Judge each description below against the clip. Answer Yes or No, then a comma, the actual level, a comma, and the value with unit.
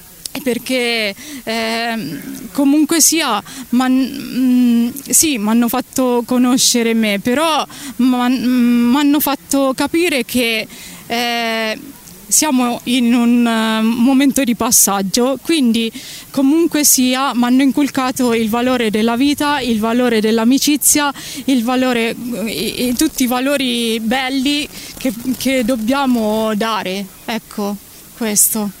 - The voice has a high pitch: Yes, very high, 250 Hz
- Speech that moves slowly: Yes, slow, 110 wpm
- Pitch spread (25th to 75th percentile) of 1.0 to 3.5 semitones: Yes, average, 2.9 semitones